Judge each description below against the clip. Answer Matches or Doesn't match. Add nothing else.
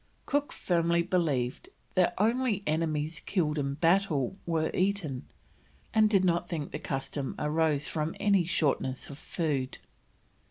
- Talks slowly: Matches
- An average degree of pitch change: Matches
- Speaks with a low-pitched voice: Doesn't match